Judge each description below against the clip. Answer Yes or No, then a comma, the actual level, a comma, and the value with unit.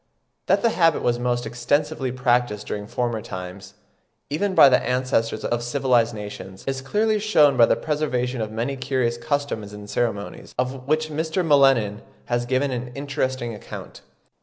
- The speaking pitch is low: Yes, low, 125 Hz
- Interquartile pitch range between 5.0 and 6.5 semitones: No, average, 3.5 semitones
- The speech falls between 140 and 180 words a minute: Yes, average, 160 wpm